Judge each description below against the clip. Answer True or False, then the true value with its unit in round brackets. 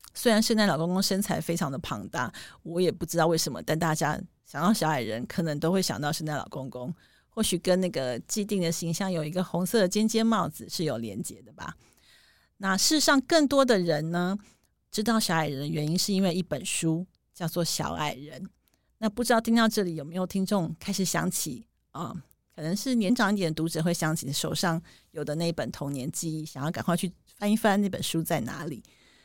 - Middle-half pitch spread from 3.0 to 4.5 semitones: True (4.2 semitones)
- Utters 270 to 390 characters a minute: True (305 characters per minute)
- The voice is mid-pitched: True (175 Hz)